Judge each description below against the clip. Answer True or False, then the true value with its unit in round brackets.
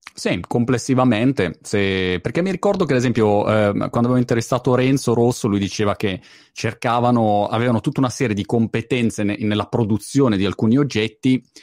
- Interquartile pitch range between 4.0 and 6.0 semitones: False (3.3 semitones)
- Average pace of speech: True (160 wpm)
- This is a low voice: True (120 Hz)